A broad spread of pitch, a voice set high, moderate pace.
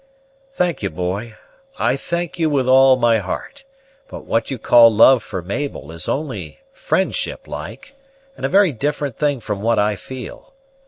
No: wide, 5.9 semitones; low, 130 Hz; average, 160 wpm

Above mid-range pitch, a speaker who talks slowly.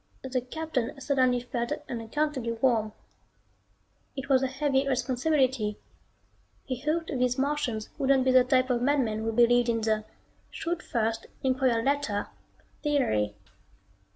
Yes: very high, 255 Hz; slow, 125 wpm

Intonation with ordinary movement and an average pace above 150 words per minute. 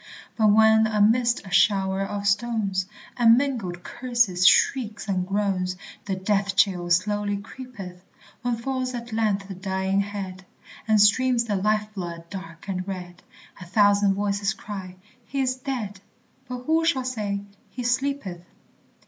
No: average, 3.7 semitones; average, 140 wpm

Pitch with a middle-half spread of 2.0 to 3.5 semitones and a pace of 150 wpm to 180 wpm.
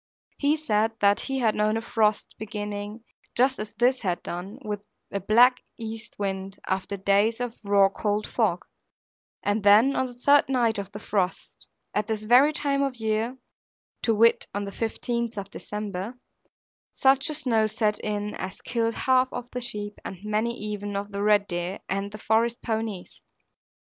Yes: average, 2.8 semitones; average, 175 wpm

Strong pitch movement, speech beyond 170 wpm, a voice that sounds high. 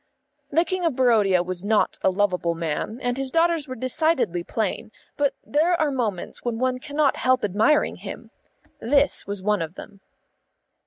No: wide, 6.5 semitones; average, 165 wpm; high, 245 Hz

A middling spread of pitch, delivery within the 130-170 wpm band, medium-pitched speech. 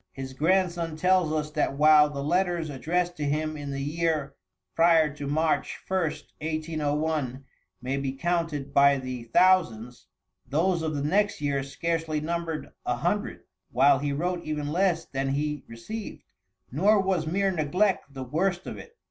Yes: average, 3.5 semitones; average, 155 wpm; medium, 155 Hz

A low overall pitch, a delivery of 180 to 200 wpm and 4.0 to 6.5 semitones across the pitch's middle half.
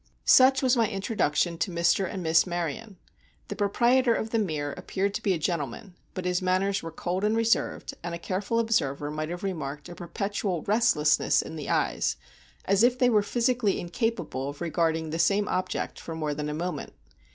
No: medium, 185 Hz; average, 190 wpm; average, 4.9 semitones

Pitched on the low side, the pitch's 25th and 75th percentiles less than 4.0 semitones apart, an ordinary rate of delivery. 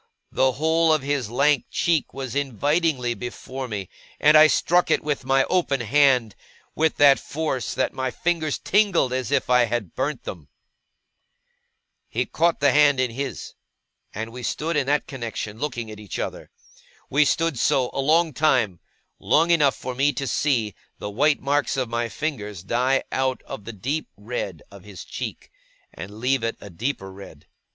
No: low, 130 Hz; average, 4.3 semitones; average, 175 wpm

